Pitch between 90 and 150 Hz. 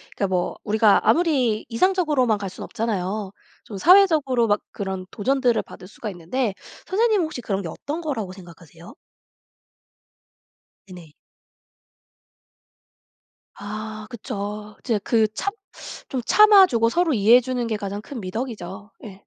No: high, 220 Hz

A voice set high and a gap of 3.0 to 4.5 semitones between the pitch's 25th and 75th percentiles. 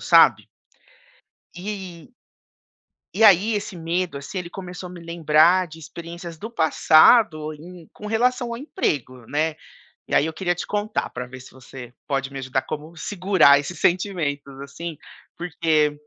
No: medium, 170 Hz; average, 3.9 semitones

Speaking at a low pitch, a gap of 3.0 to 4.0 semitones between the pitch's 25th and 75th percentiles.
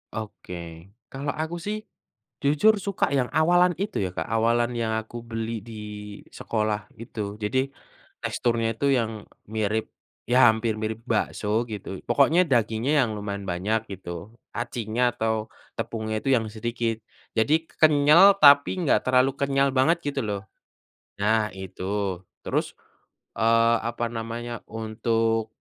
Yes: low, 115 Hz; average, 3.7 semitones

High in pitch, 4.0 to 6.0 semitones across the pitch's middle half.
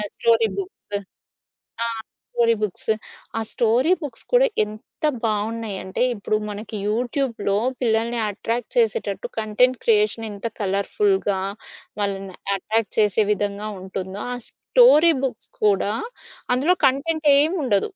Yes: high, 225 Hz; average, 4.3 semitones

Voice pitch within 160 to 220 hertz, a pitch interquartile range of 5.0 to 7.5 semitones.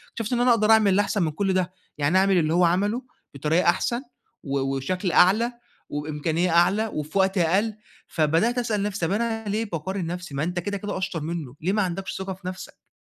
No: medium, 185 Hz; average, 3.9 semitones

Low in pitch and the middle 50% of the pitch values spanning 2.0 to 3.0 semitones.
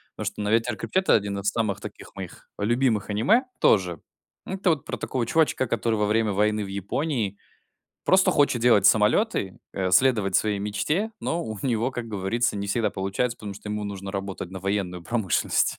No: low, 105 Hz; average, 3.6 semitones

